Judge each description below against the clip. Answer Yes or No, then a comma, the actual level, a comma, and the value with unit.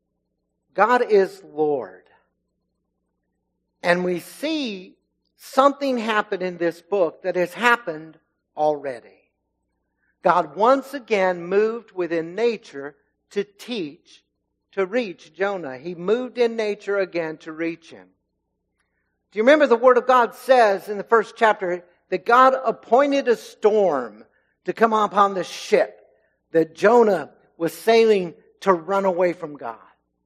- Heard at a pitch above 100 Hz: Yes, medium, 185 Hz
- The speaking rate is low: Yes, slow, 130 wpm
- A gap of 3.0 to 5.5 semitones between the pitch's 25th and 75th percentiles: No, wide, 6.2 semitones